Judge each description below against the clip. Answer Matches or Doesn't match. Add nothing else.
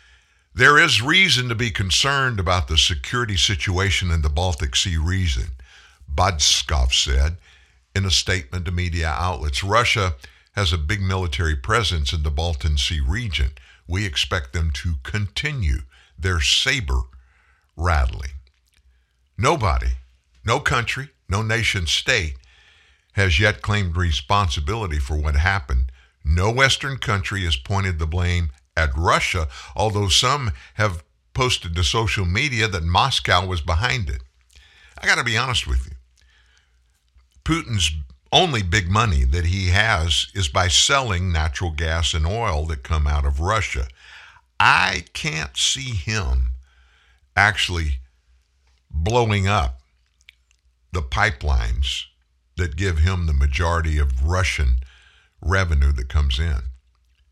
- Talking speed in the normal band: Doesn't match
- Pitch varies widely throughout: Matches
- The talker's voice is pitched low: Matches